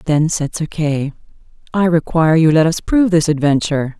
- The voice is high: No, medium, 160 Hz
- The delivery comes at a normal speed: Yes, average, 180 wpm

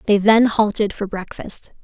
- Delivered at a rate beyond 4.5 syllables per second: No, 4.4 syllables/s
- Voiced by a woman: Yes, female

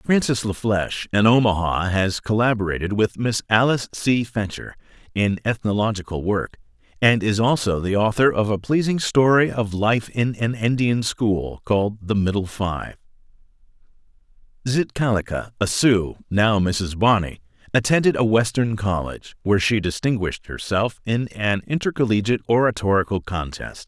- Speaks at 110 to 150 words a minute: Yes, slow, 135 wpm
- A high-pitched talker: No, low, 110 Hz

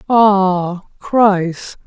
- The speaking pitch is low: No, high, 195 Hz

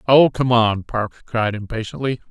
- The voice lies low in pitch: Yes, low, 115 Hz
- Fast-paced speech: No, average, 155 wpm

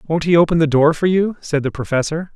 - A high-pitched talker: No, medium, 160 Hz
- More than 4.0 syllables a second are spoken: Yes, 5.7 syllables/s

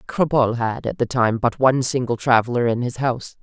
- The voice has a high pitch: No, low, 125 Hz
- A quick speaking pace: Yes, fast, 210 wpm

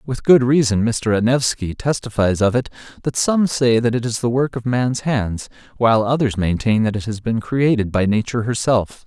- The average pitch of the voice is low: Yes, low, 120 Hz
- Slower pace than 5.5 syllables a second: Yes, 5.1 syllables/s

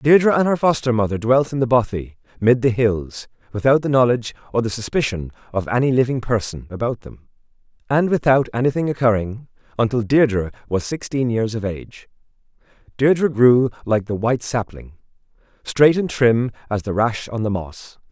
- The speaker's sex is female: No, male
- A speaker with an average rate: Yes, average, 165 wpm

